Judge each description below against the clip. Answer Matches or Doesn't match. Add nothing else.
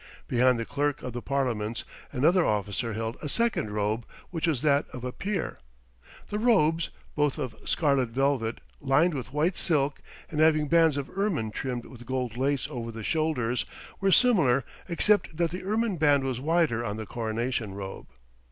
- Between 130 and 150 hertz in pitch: Matches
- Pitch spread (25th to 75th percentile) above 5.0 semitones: Matches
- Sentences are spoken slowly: Doesn't match